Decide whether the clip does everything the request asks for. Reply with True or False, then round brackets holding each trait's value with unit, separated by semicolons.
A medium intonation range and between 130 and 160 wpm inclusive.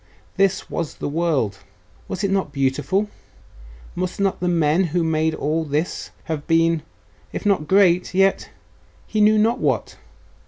True (3.9 semitones; 150 wpm)